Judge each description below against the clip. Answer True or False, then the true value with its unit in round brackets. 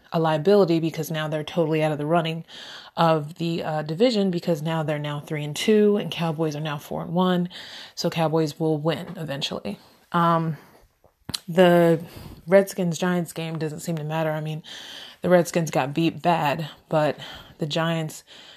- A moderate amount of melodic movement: False (1.8 semitones)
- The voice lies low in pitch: False (165 Hz)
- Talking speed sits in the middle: True (170 wpm)